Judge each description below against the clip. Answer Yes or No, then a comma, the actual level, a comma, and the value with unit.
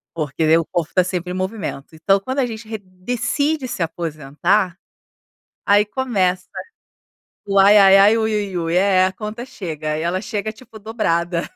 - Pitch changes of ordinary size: Yes, average, 4.1 semitones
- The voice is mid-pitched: No, high, 195 Hz